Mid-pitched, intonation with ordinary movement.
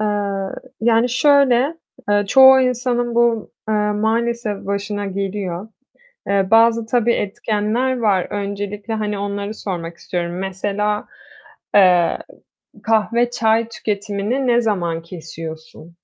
No: high, 210 Hz; average, 3.1 semitones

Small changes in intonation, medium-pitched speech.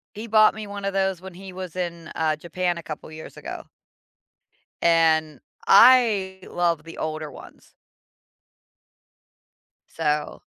No: average, 3.6 semitones; medium, 175 Hz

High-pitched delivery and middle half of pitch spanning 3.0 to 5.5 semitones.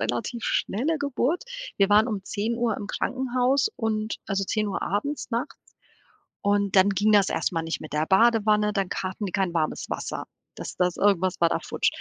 Yes: high, 210 Hz; average, 3.5 semitones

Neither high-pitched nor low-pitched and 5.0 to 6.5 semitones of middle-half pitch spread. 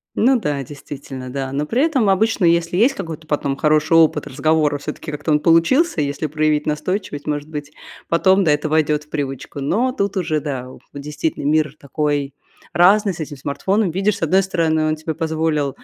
No: medium, 155 Hz; average, 3.7 semitones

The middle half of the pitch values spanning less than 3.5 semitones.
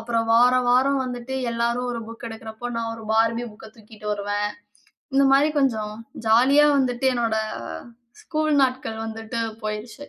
Yes: narrow, 2.5 semitones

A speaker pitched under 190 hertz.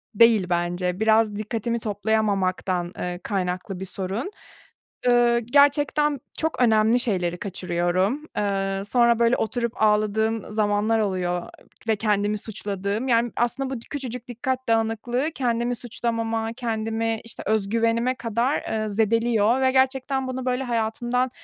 No: high, 225 Hz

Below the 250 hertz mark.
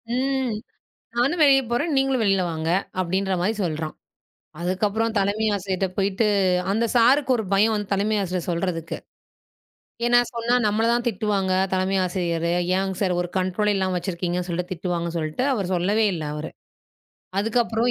Yes: high, 195 Hz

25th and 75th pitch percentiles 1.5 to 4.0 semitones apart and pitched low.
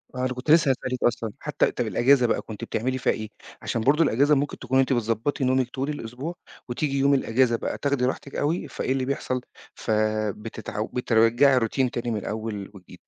Yes: average, 3.3 semitones; low, 125 Hz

